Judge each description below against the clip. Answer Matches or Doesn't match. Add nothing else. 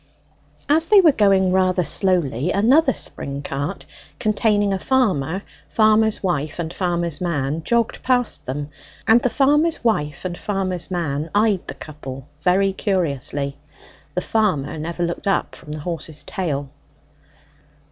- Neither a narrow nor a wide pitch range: Doesn't match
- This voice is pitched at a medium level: Matches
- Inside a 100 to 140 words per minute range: Matches